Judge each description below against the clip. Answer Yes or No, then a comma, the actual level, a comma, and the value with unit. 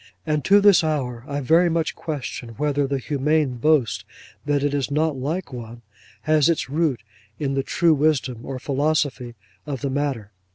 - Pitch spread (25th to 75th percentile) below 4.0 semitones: Yes, average, 3.0 semitones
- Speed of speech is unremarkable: Yes, average, 170 wpm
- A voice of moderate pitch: Yes, medium, 145 Hz